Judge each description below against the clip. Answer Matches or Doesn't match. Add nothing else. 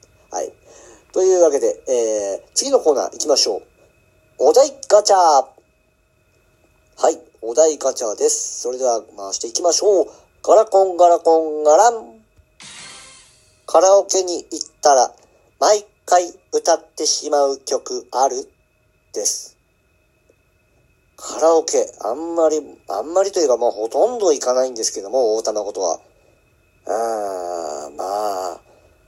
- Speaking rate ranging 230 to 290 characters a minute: Matches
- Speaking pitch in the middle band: Matches